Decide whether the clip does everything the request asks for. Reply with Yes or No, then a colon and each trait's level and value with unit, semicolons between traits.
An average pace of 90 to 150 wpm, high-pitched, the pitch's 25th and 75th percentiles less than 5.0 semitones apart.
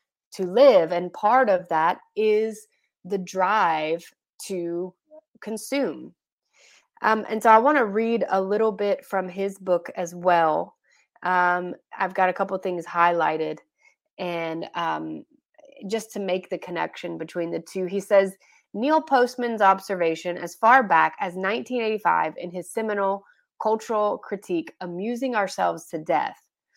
Yes: average, 140 wpm; high, 195 Hz; average, 3.9 semitones